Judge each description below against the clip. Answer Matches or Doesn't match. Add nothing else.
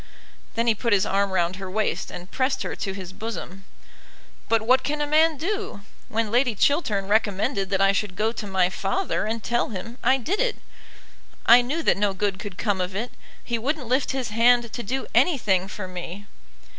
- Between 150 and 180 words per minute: Doesn't match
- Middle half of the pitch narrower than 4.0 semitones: Doesn't match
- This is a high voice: Matches